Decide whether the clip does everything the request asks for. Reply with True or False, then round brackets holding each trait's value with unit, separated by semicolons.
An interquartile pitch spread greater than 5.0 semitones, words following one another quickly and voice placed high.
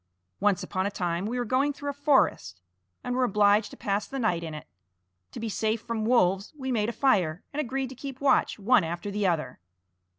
True (5.5 semitones; 220 wpm; 215 Hz)